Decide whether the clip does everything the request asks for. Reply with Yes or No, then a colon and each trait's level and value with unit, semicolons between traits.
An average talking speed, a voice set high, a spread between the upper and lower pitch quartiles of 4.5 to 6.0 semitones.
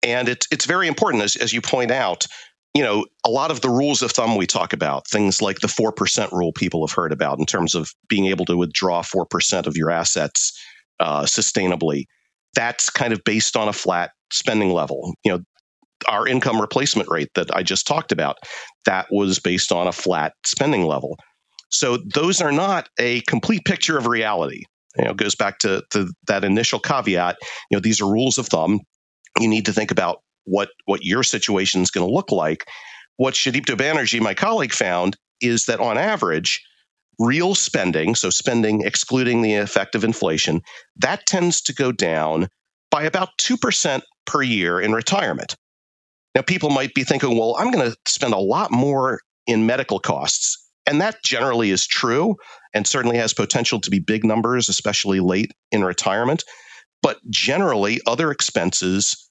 No: average, 180 wpm; low, 110 Hz; average, 5.3 semitones